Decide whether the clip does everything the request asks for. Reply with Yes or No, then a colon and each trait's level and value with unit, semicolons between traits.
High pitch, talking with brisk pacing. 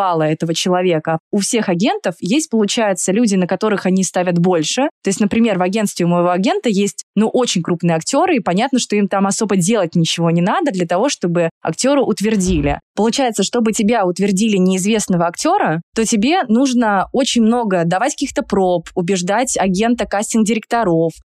Yes: high, 200 Hz; fast, 165 wpm